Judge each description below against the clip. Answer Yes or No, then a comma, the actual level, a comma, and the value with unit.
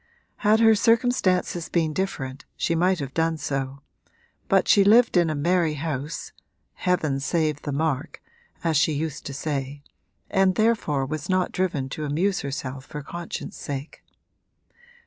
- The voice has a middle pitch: Yes, medium, 160 Hz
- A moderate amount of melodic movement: Yes, average, 4.5 semitones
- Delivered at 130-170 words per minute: Yes, average, 145 wpm